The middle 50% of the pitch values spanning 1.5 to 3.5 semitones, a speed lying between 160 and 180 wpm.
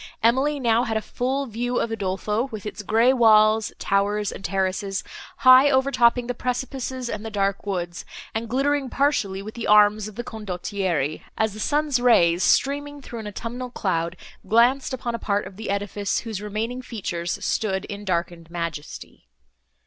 No: average, 4.0 semitones; average, 170 wpm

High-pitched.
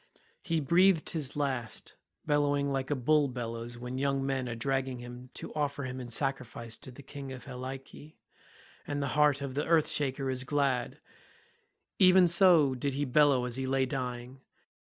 No: low, 135 Hz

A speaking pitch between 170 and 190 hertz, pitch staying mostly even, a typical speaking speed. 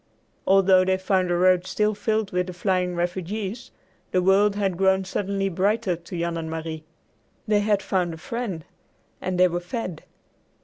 Yes: medium, 185 Hz; narrow, 2.2 semitones; average, 170 wpm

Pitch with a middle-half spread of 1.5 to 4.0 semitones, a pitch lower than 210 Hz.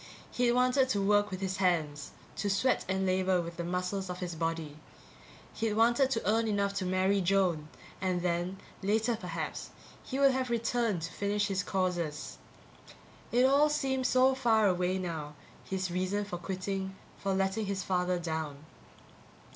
Yes: average, 3.7 semitones; high, 190 Hz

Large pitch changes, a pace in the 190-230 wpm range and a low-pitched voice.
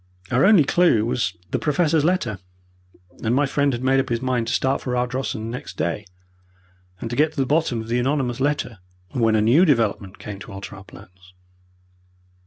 No: average, 4.3 semitones; average, 195 wpm; low, 125 Hz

